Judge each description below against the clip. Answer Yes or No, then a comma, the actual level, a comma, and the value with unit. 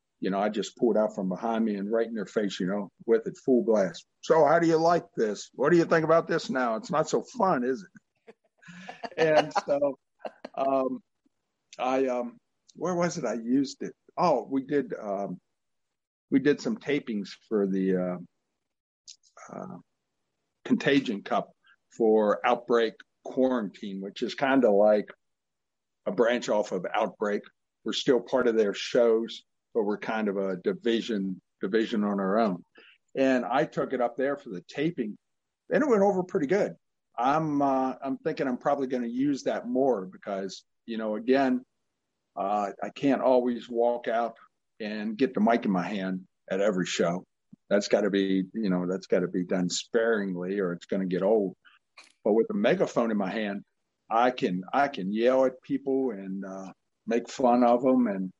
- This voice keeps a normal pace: Yes, average, 185 wpm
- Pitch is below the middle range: Yes, low, 120 Hz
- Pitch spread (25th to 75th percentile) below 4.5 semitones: No, wide, 5.4 semitones